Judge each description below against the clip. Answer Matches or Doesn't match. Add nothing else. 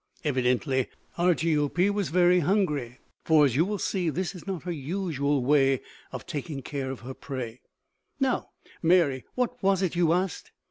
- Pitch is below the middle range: Doesn't match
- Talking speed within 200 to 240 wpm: Doesn't match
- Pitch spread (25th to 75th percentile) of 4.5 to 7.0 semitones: Matches